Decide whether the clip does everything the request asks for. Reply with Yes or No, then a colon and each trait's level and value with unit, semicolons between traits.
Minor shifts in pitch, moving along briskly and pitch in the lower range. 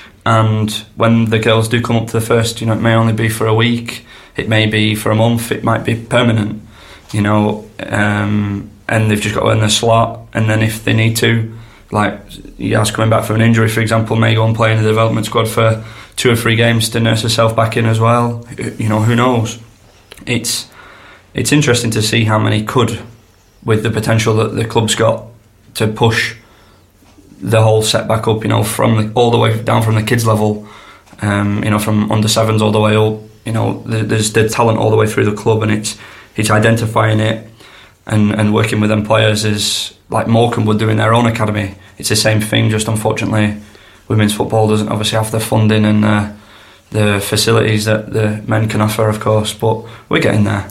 Yes: narrow, 1.1 semitones; fast, 215 wpm; low, 110 Hz